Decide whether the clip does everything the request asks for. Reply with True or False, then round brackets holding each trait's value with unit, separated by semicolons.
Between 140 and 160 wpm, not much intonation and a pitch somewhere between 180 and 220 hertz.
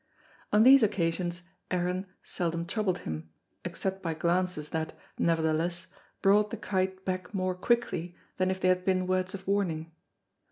True (150 wpm; 2.2 semitones; 185 Hz)